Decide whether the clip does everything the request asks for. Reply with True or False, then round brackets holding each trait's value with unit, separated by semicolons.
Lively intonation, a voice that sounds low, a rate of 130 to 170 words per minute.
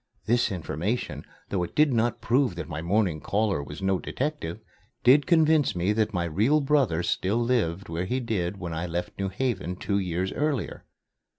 False (6.1 semitones; 100 Hz; 180 wpm)